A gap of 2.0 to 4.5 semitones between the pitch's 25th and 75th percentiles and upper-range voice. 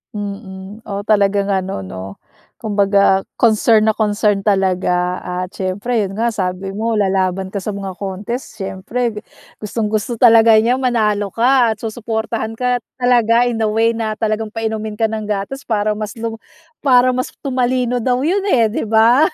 Yes: average, 2.8 semitones; high, 215 Hz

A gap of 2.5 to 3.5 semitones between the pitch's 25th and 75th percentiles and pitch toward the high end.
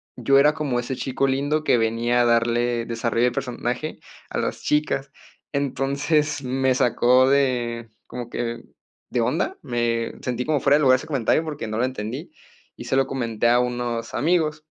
No: average, 2.8 semitones; low, 125 Hz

